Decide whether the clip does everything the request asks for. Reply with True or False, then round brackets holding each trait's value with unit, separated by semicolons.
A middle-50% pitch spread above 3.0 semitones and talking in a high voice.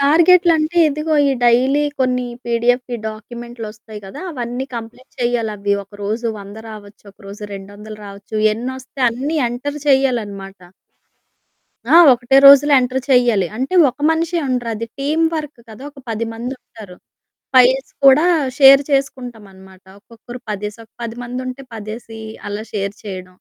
True (4.1 semitones; 240 Hz)